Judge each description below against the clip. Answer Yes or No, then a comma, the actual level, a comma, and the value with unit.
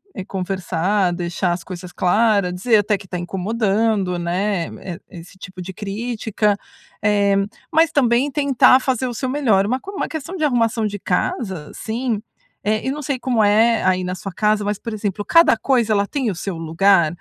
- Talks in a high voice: Yes, high, 210 Hz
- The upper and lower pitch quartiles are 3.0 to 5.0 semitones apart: Yes, average, 4.3 semitones